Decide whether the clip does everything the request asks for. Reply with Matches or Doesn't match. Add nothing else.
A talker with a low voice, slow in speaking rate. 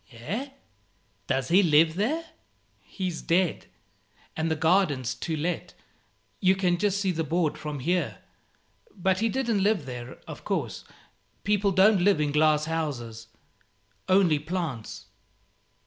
Doesn't match